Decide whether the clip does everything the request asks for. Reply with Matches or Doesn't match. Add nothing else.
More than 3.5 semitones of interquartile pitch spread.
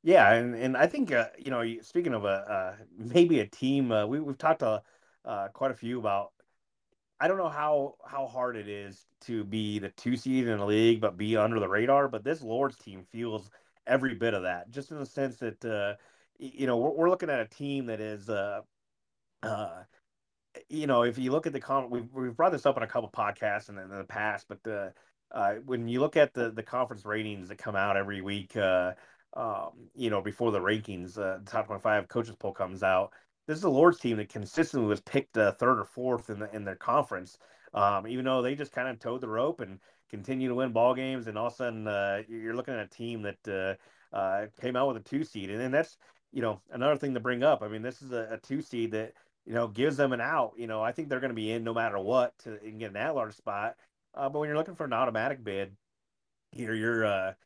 Matches